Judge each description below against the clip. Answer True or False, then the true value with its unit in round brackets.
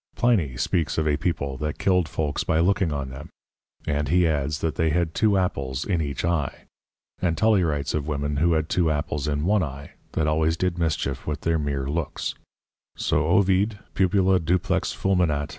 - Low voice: True (80 Hz)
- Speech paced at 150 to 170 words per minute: False (185 wpm)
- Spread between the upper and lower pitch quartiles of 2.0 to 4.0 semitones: True (3.7 semitones)